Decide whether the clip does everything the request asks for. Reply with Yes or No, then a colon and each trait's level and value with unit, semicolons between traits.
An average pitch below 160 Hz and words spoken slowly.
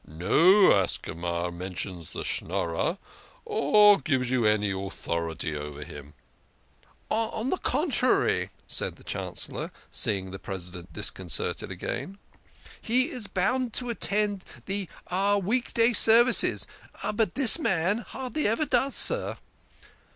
No: medium, 185 Hz; slow, 125 wpm